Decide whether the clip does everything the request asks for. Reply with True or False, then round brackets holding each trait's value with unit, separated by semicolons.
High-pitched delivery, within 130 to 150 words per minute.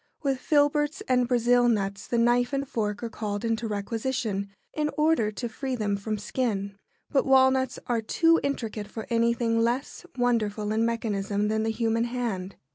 False (230 Hz; 165 wpm)